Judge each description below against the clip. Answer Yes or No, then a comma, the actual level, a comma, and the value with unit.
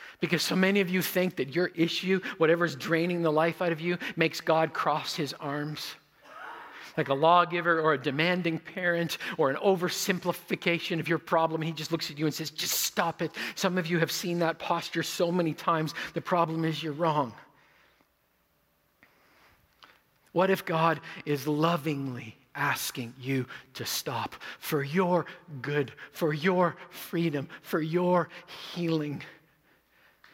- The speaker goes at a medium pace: Yes, average, 155 wpm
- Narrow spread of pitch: Yes, narrow, 2.2 semitones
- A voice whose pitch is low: No, medium, 165 Hz